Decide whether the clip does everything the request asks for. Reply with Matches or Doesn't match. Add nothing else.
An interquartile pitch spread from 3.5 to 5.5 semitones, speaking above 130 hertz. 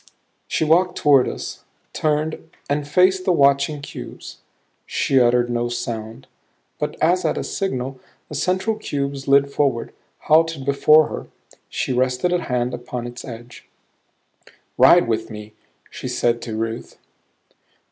Matches